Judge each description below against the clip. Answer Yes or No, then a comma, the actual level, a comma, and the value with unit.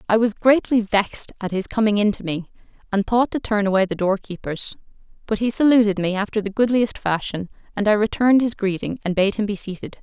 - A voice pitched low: No, high, 210 Hz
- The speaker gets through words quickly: Yes, fast, 210 wpm